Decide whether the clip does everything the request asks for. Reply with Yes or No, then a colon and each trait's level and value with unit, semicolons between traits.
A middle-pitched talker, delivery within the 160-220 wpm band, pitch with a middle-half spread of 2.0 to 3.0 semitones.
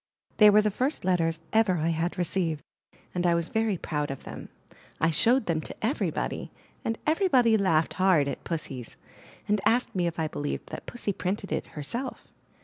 No: medium, 180 Hz; average, 180 wpm; wide, 5.4 semitones